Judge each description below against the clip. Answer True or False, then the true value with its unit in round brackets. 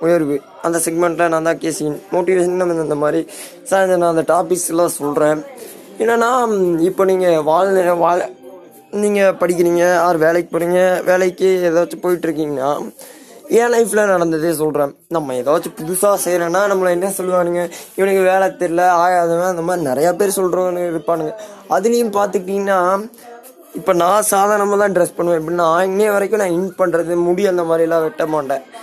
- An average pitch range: False (2.3 semitones)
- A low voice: False (175 Hz)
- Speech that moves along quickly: True (140 wpm)